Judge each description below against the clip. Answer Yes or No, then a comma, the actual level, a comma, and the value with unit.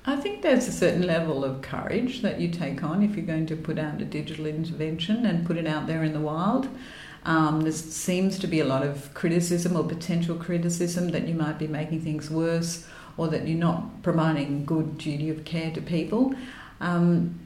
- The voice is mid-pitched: Yes, medium, 165 Hz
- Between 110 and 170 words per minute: No, fast, 205 wpm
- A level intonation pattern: Yes, narrow, 2.0 semitones